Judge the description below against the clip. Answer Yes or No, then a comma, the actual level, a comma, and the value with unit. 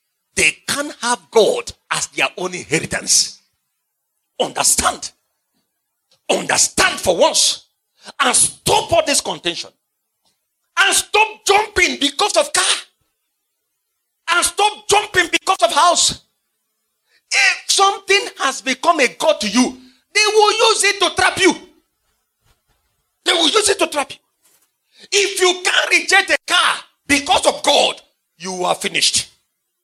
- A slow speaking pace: Yes, slow, 125 wpm